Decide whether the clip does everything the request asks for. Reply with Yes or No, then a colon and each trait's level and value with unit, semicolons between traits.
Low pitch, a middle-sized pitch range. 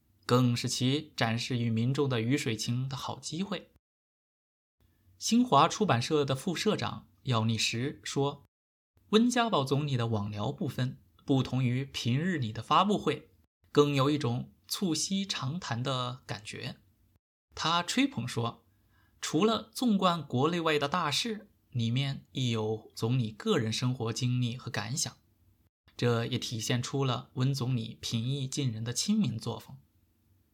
Yes: low, 125 Hz; average, 4.7 semitones